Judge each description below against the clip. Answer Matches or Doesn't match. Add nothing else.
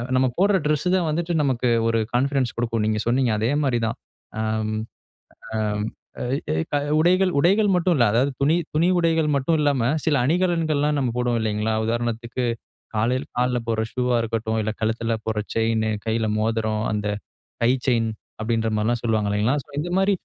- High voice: Doesn't match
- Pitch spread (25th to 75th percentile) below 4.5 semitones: Doesn't match